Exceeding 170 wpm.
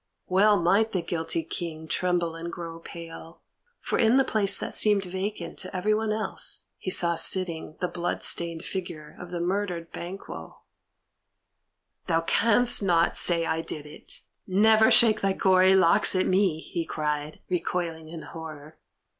No: average, 155 wpm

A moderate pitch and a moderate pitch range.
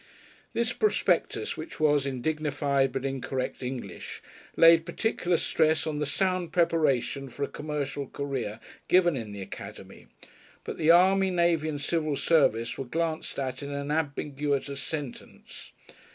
Yes: medium, 150 Hz; average, 3.3 semitones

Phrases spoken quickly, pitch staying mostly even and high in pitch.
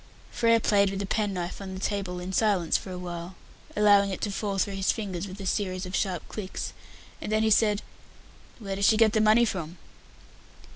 Yes: fast, 210 wpm; narrow, 2.3 semitones; high, 200 Hz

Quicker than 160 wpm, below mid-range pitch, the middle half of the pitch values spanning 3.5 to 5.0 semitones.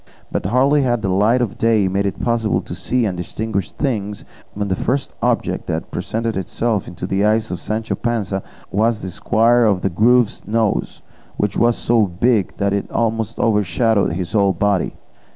No: average, 180 wpm; low, 110 Hz; average, 2.9 semitones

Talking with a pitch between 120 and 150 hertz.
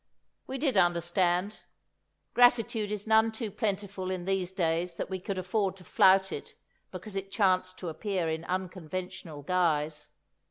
No: medium, 185 Hz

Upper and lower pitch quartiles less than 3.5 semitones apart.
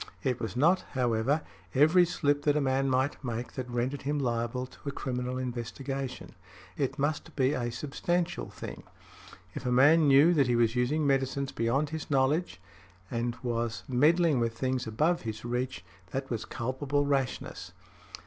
Yes: average, 3.0 semitones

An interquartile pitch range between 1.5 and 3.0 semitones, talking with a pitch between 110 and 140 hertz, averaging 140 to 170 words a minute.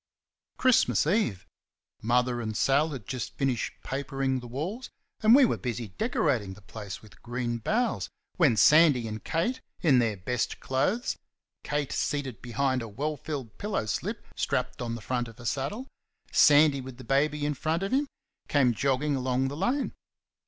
No: average, 4.4 semitones; low, 135 Hz; average, 165 wpm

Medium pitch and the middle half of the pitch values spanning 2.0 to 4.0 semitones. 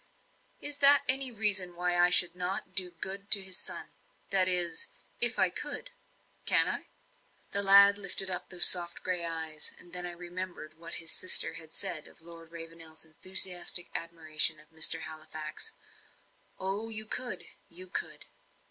Yes: medium, 180 Hz; average, 2.8 semitones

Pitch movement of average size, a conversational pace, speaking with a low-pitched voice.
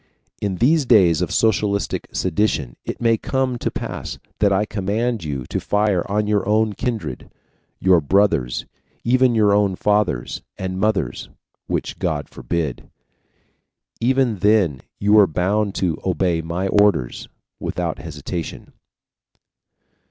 No: average, 3.6 semitones; slow, 130 wpm; low, 100 Hz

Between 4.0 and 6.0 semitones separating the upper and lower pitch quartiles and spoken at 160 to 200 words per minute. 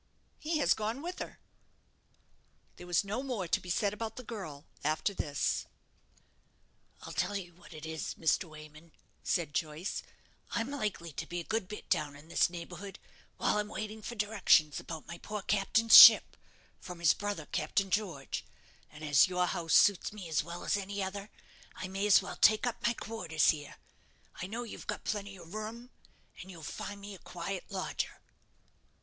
Yes: average, 4.3 semitones; average, 180 wpm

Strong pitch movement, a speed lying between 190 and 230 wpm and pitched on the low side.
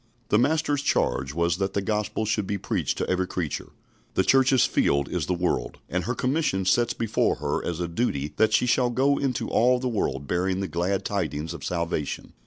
Yes: wide, 6.3 semitones; average, 200 wpm; very low, 95 Hz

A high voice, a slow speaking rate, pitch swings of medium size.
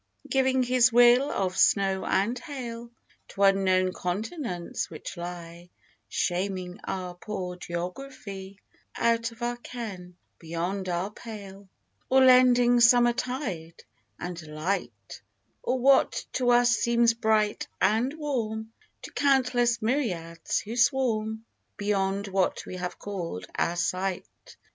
Yes: high, 210 Hz; slow, 125 wpm; average, 5.0 semitones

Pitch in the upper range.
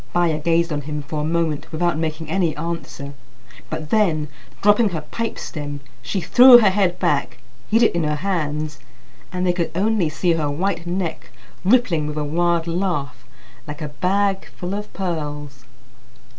No: medium, 165 Hz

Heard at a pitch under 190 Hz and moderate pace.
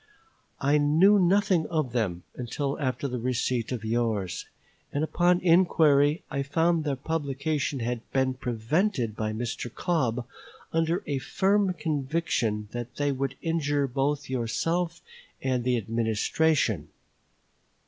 No: medium, 140 Hz; slow, 125 wpm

